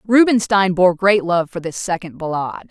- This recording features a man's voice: No, female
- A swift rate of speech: No, average, 175 wpm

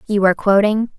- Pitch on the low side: No, high, 205 Hz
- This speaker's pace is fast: No, average, 185 wpm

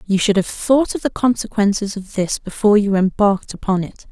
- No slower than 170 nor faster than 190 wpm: No, fast, 205 wpm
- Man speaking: No, female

